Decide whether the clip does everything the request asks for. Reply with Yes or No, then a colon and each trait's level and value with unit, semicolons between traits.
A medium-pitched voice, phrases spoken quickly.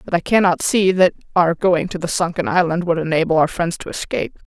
Yes: medium, 170 Hz; fast, 225 wpm